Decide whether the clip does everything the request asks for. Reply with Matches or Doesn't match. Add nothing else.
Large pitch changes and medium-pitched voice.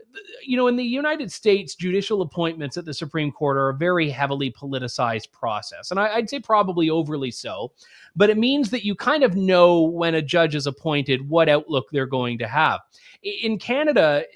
Matches